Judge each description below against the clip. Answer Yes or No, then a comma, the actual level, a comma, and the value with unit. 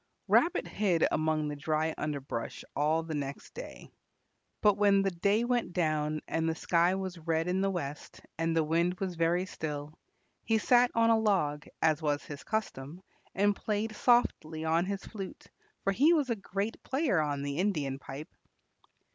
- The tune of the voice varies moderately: Yes, average, 4.8 semitones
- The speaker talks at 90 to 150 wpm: No, average, 170 wpm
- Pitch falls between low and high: Yes, medium, 170 Hz